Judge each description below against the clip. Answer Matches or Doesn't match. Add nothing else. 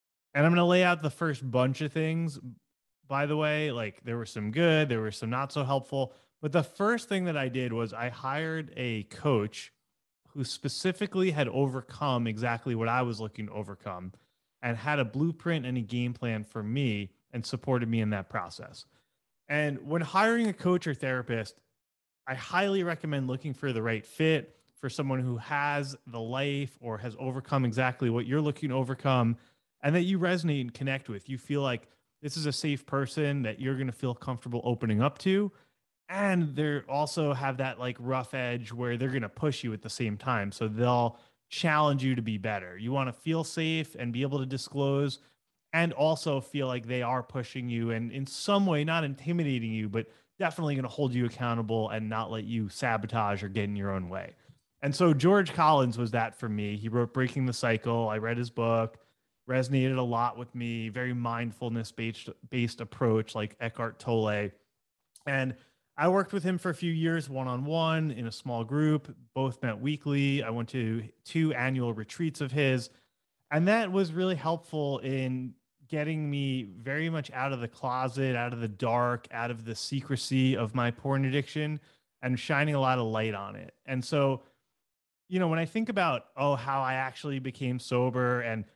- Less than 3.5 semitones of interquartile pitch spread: Doesn't match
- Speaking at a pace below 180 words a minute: Doesn't match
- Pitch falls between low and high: Doesn't match